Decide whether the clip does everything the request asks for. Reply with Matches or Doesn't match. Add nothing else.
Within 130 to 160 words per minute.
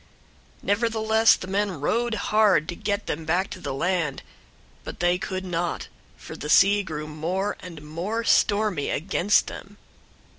Matches